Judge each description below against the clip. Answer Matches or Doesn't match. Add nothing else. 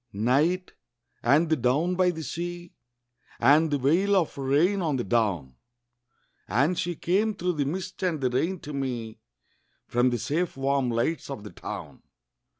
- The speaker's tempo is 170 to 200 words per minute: Doesn't match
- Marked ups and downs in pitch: Matches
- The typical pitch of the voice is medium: Matches